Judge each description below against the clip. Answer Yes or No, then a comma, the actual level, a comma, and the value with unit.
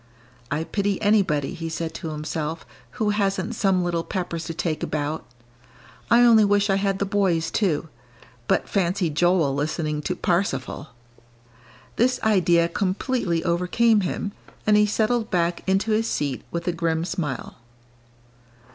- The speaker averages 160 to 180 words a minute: No, average, 145 wpm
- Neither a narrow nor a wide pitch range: Yes, average, 4.0 semitones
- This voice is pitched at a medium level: Yes, medium, 180 Hz